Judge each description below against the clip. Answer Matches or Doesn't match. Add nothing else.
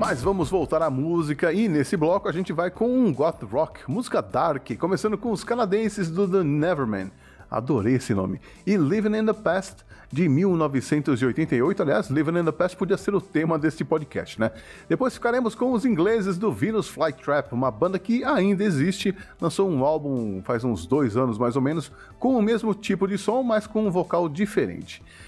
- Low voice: Doesn't match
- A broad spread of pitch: Matches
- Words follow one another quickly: Matches